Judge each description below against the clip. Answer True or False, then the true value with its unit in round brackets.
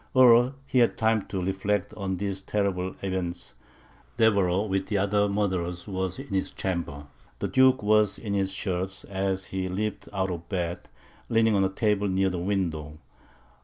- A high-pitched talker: False (95 Hz)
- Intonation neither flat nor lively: False (2.0 semitones)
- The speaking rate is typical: True (175 wpm)